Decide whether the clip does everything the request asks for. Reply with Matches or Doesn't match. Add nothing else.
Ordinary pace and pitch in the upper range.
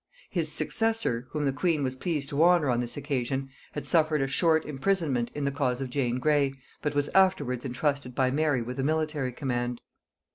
Doesn't match